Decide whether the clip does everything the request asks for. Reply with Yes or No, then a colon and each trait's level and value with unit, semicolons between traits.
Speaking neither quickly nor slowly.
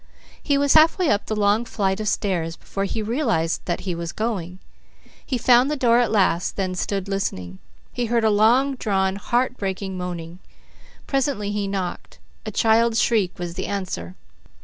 Yes: average, 170 wpm